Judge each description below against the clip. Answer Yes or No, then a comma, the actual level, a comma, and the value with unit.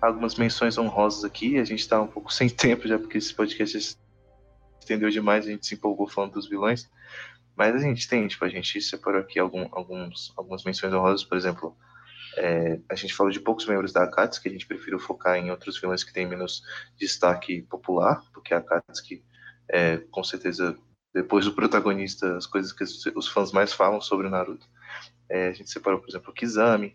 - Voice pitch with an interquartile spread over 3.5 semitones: No, average, 3.1 semitones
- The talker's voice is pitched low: Yes, low, 100 Hz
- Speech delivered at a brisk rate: Yes, fast, 195 wpm